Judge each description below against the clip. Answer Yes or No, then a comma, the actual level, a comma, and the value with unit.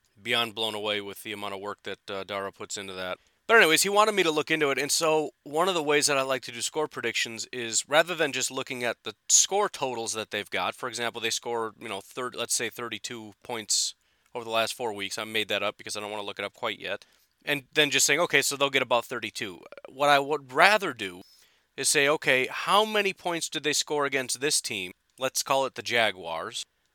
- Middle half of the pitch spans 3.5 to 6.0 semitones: Yes, average, 4.8 semitones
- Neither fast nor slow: No, fast, 245 wpm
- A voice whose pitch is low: Yes, low, 125 Hz